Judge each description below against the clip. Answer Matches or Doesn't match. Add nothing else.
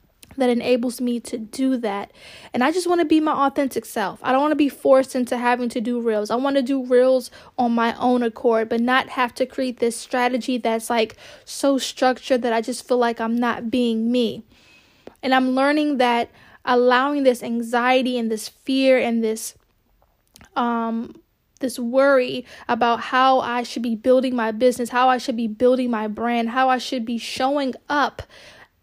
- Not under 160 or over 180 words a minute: Doesn't match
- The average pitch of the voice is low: Doesn't match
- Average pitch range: Doesn't match